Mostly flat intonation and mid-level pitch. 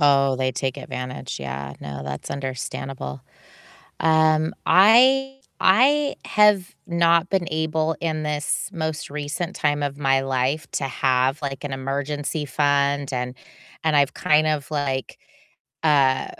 No: average, 3.1 semitones; medium, 145 Hz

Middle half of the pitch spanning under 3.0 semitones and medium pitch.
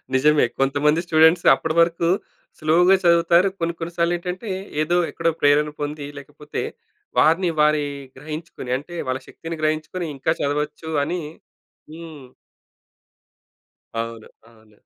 Yes: narrow, 2.4 semitones; medium, 155 Hz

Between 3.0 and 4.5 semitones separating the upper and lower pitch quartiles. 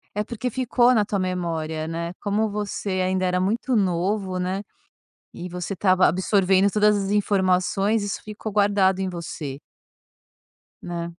No: narrow, 2.4 semitones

